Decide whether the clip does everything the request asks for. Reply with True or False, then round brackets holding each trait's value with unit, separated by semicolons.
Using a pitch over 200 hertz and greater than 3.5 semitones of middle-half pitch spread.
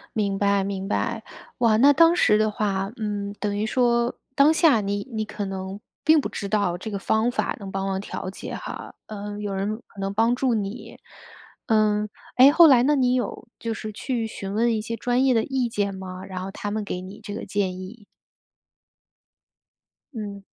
False (210 Hz; 3.1 semitones)